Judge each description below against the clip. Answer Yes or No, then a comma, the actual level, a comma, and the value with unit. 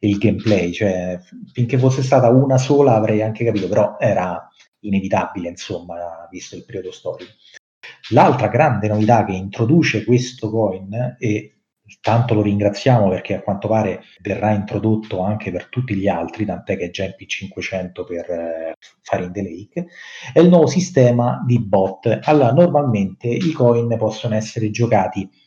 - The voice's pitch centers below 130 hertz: Yes, low, 110 Hz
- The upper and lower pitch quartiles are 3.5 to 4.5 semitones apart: Yes, average, 4.0 semitones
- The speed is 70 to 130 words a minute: No, average, 155 wpm